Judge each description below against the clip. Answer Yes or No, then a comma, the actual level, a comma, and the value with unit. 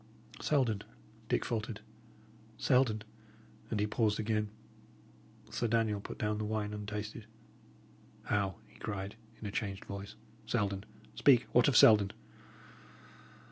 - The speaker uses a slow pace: Yes, slow, 120 wpm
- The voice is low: Yes, low, 105 Hz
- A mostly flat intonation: Yes, narrow, 1.7 semitones